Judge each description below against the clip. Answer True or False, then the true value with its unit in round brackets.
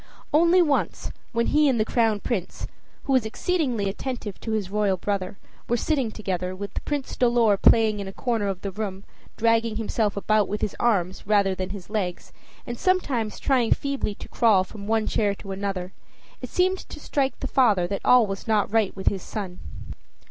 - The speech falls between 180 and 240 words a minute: True (190 wpm)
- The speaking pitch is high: True (215 Hz)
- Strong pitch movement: False (3.4 semitones)